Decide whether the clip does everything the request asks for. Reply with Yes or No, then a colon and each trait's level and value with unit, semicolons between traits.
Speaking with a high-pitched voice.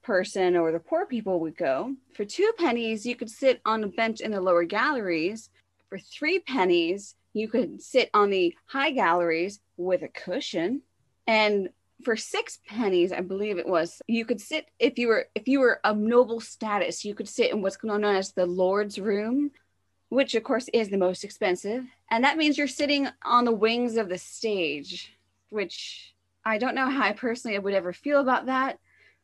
Yes: high, 225 Hz